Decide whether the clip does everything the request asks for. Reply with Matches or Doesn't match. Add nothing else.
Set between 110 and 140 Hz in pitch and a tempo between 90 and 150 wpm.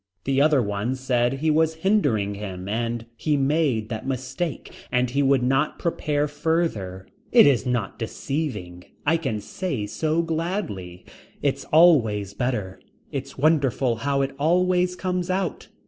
Matches